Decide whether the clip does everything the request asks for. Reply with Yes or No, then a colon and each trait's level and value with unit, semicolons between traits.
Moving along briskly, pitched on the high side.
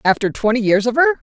Yes: fast, 230 wpm; high, 240 Hz